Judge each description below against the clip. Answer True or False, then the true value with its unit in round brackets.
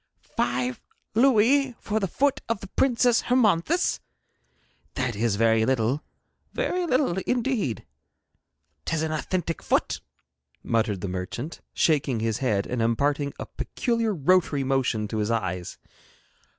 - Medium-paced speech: False (125 wpm)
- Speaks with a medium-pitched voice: True (145 Hz)